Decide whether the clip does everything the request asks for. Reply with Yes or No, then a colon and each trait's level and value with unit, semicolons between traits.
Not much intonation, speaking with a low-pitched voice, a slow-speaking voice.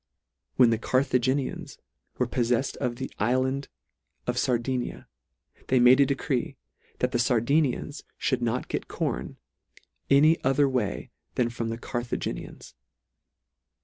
Yes: narrow, 2.0 semitones; low, 125 Hz; slow, 120 wpm